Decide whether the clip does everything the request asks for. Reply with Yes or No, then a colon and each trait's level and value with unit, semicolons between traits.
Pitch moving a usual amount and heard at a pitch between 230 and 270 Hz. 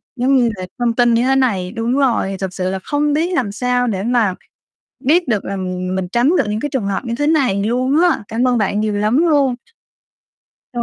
Yes: average, 4.7 semitones; high, 235 Hz